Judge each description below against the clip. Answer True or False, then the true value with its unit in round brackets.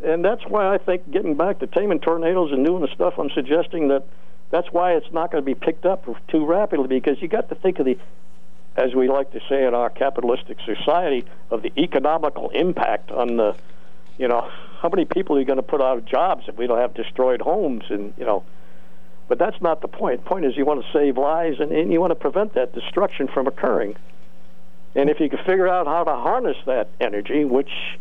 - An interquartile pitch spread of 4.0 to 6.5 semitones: True (4.9 semitones)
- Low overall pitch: False (160 Hz)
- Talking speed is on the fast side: True (230 wpm)